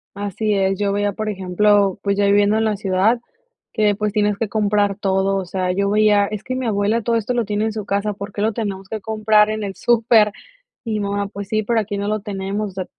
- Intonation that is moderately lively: No, narrow, 1.4 semitones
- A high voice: Yes, high, 205 Hz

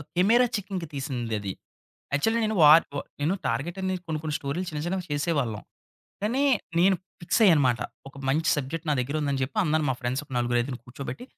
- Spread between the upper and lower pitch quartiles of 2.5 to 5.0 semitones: No, wide, 5.5 semitones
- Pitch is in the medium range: Yes, medium, 150 Hz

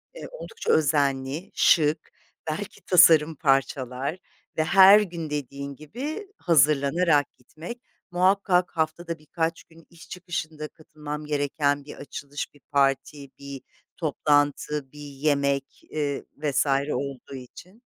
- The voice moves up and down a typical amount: Yes, average, 3.3 semitones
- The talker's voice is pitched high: No, medium, 150 Hz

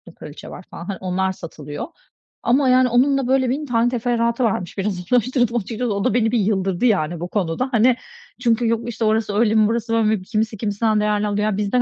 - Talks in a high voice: Yes, high, 220 Hz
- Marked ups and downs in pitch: No, average, 3.3 semitones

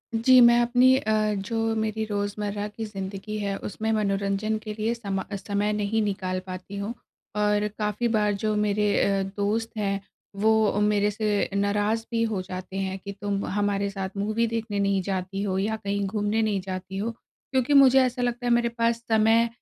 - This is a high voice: Yes, high, 210 Hz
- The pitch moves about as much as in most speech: No, narrow, 2.0 semitones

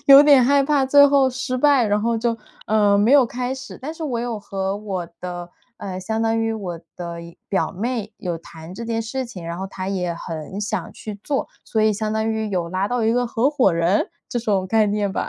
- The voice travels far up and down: No, average, 4.6 semitones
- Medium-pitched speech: No, high, 220 Hz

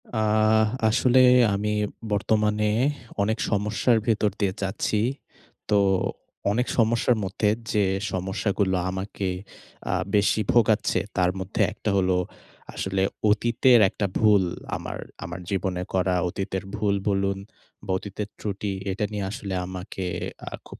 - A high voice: No, low, 105 Hz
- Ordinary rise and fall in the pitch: No, narrow, 2.1 semitones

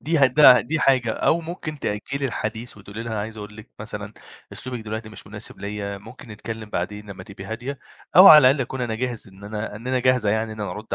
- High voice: No, low, 110 Hz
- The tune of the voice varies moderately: Yes, average, 3.5 semitones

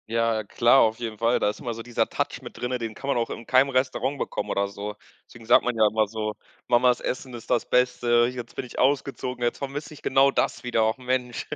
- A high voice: No, low, 120 Hz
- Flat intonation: Yes, narrow, 2.1 semitones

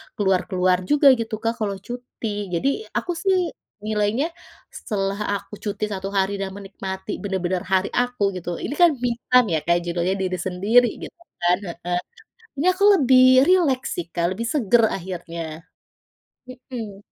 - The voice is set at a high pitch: Yes, high, 200 Hz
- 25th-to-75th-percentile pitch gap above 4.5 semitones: Yes, average, 4.9 semitones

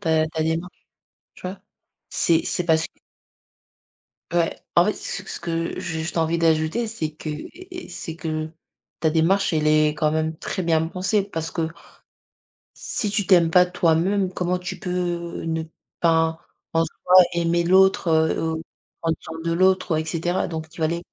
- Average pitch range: No, narrow, 2.2 semitones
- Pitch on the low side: No, medium, 165 Hz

